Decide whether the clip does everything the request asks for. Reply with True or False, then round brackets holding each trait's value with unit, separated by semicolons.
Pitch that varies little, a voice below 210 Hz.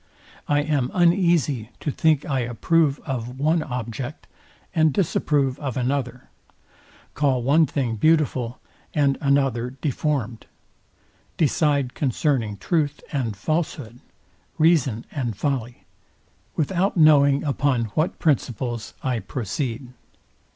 False (3.8 semitones; 140 Hz)